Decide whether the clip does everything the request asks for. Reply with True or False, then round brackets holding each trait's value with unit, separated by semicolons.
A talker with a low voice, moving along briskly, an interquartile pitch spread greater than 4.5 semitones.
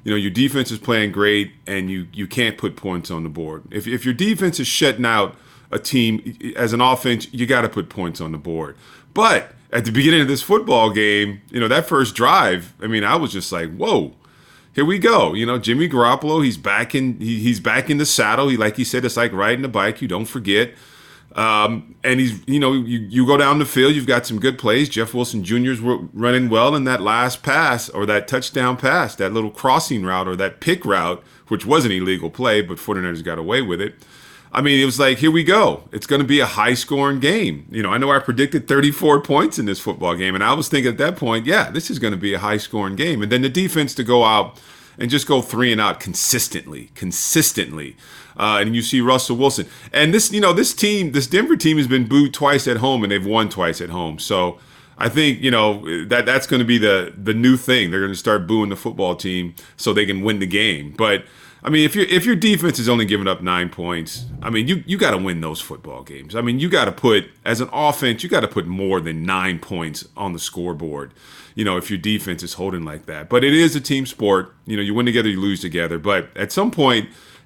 True (120 Hz; 245 wpm; 5.3 semitones)